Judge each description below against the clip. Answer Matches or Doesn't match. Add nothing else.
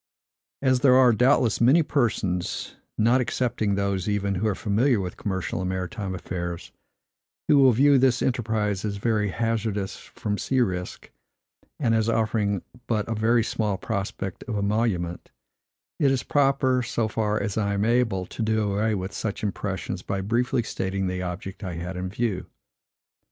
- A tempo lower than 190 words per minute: Matches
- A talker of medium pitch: Doesn't match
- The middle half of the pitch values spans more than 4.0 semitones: Doesn't match